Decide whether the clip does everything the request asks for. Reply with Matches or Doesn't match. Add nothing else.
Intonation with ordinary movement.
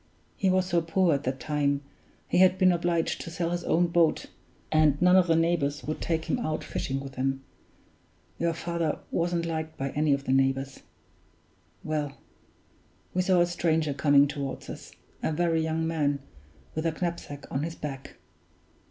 Matches